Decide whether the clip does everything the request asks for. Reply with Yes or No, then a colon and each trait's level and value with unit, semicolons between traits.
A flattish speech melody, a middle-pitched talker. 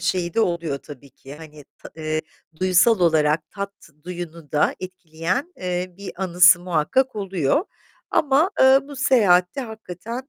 No: wide, 5.4 semitones; medium, 180 Hz